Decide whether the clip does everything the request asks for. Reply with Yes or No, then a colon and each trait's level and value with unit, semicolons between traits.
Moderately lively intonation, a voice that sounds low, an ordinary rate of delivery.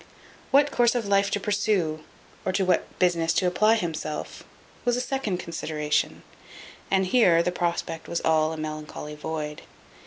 No: average, 4.5 semitones; medium, 175 Hz; average, 155 wpm